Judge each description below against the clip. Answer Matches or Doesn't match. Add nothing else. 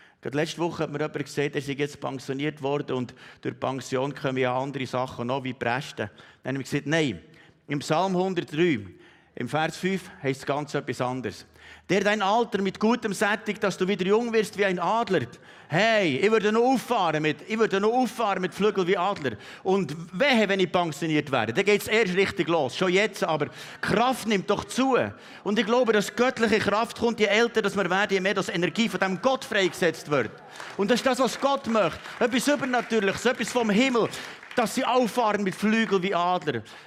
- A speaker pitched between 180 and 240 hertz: Matches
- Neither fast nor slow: Doesn't match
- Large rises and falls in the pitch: Matches